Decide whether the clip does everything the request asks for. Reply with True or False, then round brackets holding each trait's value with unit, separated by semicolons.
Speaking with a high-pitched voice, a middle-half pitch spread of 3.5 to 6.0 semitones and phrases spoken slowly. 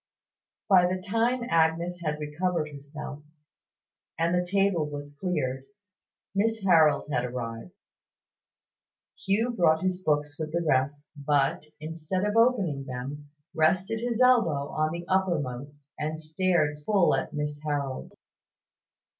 False (155 Hz; 4.3 semitones; 125 wpm)